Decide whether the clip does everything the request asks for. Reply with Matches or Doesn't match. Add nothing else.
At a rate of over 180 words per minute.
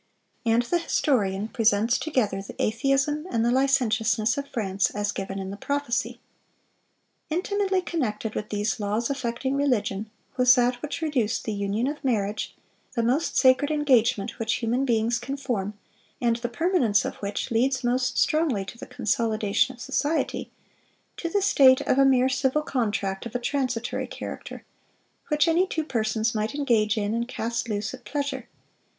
Doesn't match